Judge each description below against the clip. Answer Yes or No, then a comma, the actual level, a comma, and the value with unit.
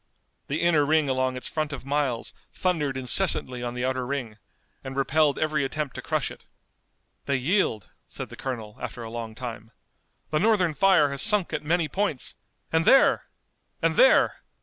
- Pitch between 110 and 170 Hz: Yes, medium, 140 Hz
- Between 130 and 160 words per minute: No, average, 170 wpm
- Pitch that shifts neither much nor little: Yes, average, 3.9 semitones